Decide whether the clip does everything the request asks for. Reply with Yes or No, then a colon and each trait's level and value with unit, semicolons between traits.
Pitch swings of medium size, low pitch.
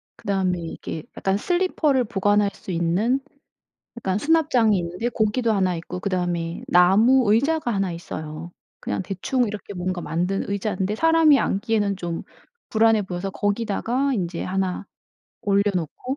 No: average, 4.4 semitones; high, 200 Hz